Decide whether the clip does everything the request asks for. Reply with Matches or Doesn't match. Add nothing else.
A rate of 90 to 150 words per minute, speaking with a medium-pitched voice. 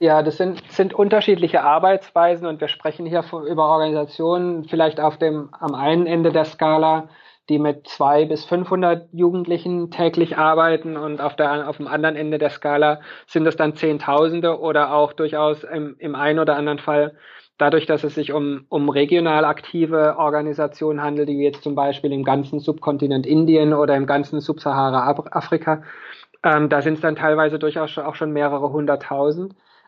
Doesn't match